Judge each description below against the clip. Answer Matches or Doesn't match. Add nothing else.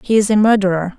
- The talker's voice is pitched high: Matches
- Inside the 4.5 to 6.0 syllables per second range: Doesn't match